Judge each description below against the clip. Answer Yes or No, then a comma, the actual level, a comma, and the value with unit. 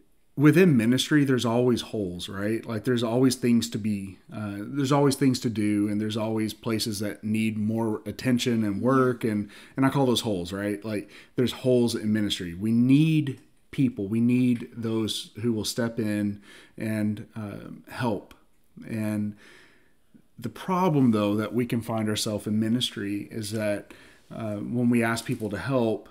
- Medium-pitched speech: No, low, 110 Hz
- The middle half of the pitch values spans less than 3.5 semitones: Yes, average, 2.9 semitones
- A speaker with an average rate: Yes, average, 170 wpm